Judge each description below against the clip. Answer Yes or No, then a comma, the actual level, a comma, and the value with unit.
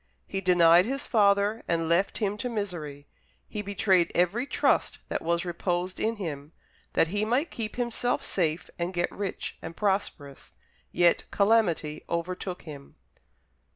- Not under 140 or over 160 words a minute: Yes, average, 145 wpm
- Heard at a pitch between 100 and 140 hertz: No, medium, 185 Hz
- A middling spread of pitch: Yes, average, 3.6 semitones